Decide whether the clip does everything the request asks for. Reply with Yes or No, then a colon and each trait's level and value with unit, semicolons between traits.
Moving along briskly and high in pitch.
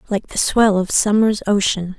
No: average, 180 wpm; high, 205 Hz